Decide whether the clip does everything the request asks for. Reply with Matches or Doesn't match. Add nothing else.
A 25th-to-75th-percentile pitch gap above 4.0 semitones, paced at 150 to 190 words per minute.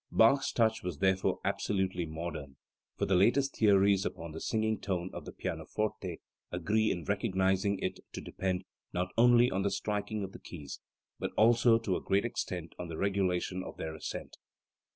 Doesn't match